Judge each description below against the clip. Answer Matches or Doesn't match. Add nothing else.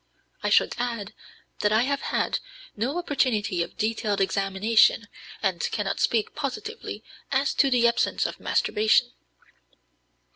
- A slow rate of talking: Matches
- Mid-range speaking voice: Doesn't match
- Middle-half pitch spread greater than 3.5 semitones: Matches